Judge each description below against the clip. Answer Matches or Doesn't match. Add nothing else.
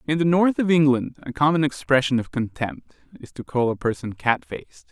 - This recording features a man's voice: Matches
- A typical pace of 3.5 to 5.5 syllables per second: Doesn't match